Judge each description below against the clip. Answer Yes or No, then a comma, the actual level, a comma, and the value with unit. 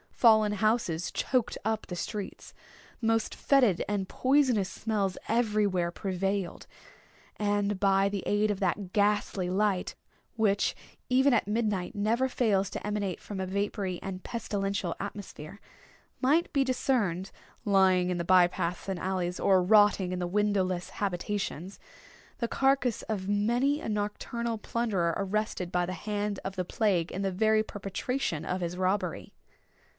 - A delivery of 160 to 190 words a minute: No, average, 145 wpm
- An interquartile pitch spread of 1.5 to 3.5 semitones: Yes, average, 2.8 semitones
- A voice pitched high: Yes, high, 205 Hz